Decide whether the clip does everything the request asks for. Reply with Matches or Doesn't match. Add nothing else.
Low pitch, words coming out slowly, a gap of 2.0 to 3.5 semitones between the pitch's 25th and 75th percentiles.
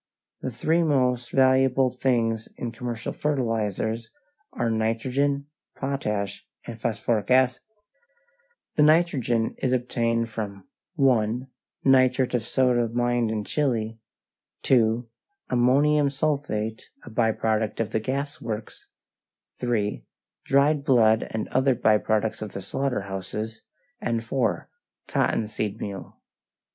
Matches